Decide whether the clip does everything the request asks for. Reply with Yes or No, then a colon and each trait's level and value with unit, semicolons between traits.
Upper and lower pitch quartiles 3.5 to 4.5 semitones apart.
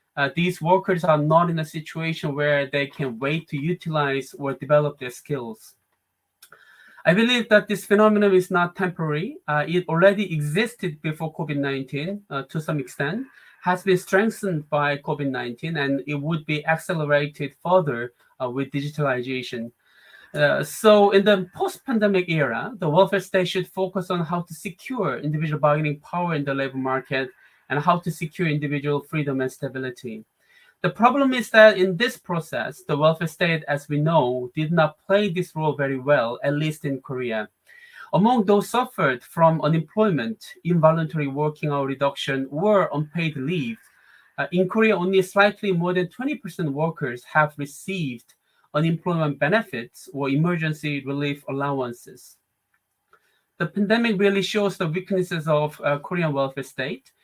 No: average, 4.9 semitones